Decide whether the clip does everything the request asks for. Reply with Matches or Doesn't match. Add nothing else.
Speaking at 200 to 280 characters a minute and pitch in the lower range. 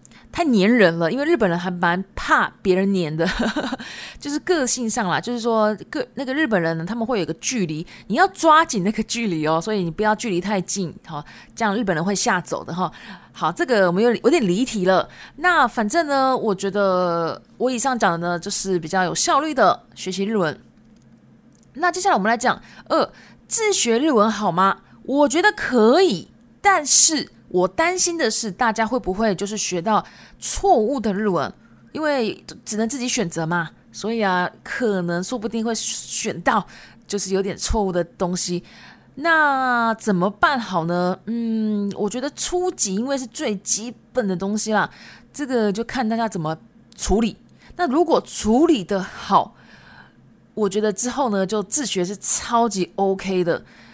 Doesn't match